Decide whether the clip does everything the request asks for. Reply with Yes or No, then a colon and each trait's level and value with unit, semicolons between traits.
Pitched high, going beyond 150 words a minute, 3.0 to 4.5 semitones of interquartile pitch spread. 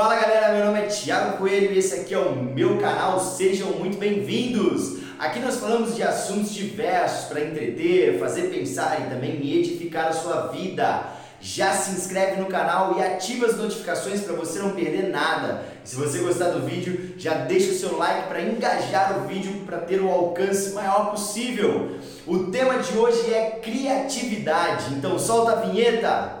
Yes: high, 195 Hz; average, 175 wpm; average, 3.8 semitones